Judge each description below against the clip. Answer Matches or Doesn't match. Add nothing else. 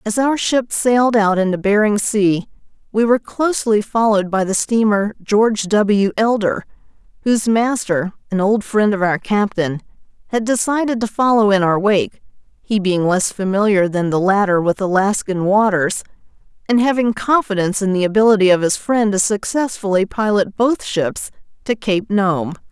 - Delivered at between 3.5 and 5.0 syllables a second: Matches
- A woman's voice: Matches